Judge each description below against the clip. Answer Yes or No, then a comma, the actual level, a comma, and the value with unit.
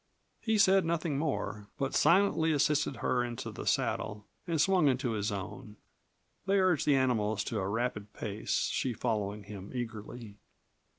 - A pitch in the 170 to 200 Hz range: No, low, 125 Hz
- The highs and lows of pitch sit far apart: Yes, wide, 6.9 semitones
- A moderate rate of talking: Yes, average, 155 wpm